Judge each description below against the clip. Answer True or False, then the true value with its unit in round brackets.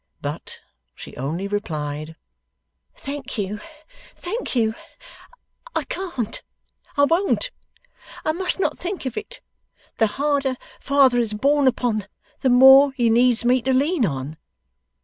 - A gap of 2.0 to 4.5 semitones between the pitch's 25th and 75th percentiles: False (5.2 semitones)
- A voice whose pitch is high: True (255 Hz)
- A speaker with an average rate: False (130 wpm)